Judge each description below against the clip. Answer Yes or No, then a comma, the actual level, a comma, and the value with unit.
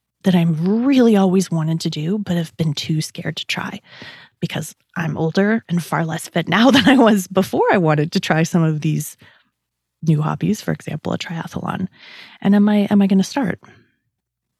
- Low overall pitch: No, medium, 175 Hz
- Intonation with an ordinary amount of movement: Yes, average, 4.0 semitones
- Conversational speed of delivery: Yes, average, 190 wpm